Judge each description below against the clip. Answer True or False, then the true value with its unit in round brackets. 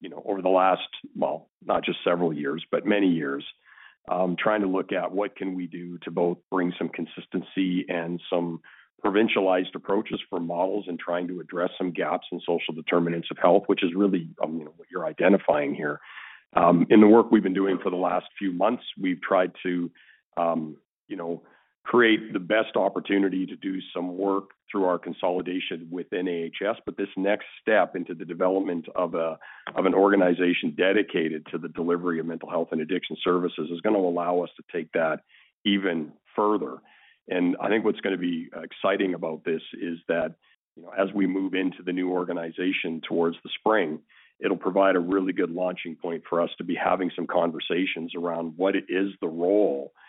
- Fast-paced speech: False (195 wpm)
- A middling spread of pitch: False (1.9 semitones)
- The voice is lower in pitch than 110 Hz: True (90 Hz)